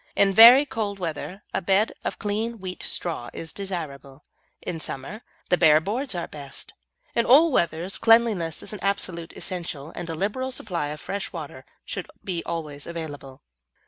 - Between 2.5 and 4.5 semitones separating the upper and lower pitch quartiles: No, average, 4.9 semitones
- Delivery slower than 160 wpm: No, average, 165 wpm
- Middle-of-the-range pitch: Yes, medium, 180 Hz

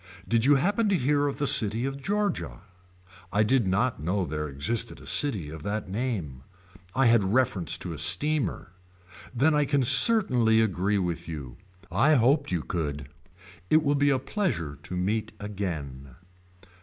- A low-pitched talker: Yes, low, 110 Hz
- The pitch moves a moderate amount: No, wide, 7.9 semitones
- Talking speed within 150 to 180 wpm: Yes, average, 165 wpm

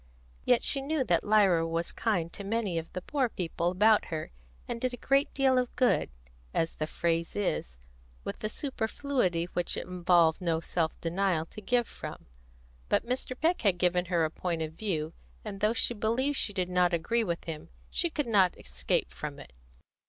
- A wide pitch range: Yes, wide, 5.8 semitones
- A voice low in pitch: No, medium, 185 Hz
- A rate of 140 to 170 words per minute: No, average, 190 wpm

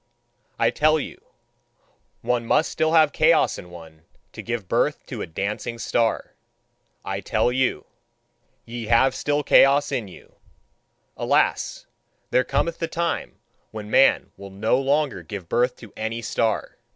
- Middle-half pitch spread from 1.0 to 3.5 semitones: No, average, 4.8 semitones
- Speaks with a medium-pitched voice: No, low, 120 Hz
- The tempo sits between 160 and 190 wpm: No, average, 145 wpm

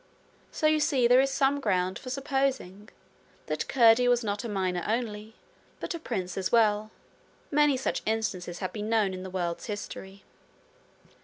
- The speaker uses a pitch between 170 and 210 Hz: No, high, 220 Hz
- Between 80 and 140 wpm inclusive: No, average, 165 wpm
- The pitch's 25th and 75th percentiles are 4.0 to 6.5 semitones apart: Yes, average, 5.2 semitones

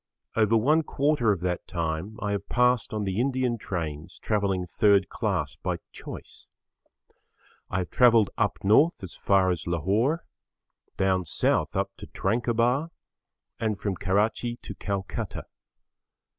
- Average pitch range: Yes, average, 4.1 semitones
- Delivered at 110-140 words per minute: Yes, slow, 135 wpm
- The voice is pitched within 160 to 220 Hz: No, low, 105 Hz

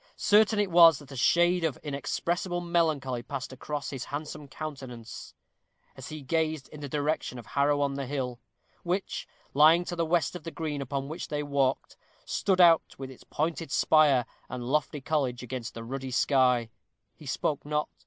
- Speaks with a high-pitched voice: No, medium, 145 Hz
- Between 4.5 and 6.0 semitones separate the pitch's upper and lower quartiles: No, average, 3.5 semitones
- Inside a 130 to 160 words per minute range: No, average, 175 wpm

